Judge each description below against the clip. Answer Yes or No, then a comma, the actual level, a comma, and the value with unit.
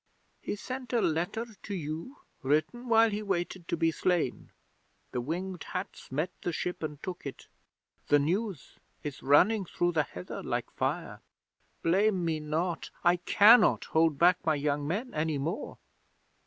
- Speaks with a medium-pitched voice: Yes, medium, 175 Hz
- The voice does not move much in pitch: No, average, 4.7 semitones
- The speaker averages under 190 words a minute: Yes, average, 155 wpm